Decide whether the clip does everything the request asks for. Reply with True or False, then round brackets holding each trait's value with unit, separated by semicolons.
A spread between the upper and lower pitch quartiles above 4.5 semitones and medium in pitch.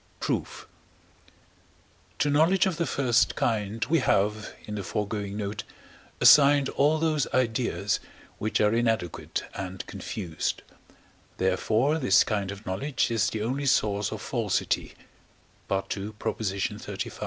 False (5.5 semitones; 110 Hz)